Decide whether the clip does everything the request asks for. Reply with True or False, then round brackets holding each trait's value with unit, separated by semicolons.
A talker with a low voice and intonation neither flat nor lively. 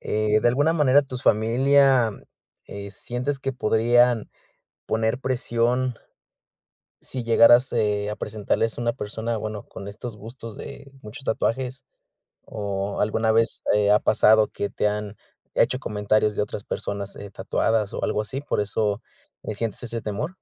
True (115 Hz; 3.0 semitones)